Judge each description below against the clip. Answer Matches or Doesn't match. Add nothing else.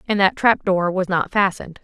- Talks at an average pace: Doesn't match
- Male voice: Doesn't match